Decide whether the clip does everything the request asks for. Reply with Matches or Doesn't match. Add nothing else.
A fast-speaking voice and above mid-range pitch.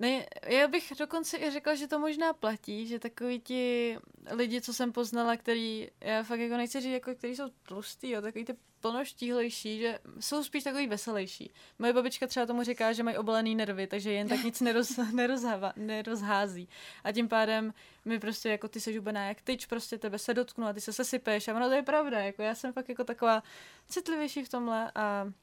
Matches